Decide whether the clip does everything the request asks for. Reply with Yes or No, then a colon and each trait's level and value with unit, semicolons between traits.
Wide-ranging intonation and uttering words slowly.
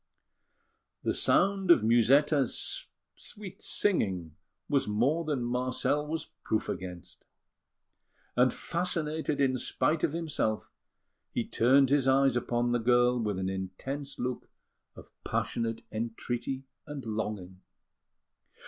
No: average, 4.6 semitones; slow, 110 wpm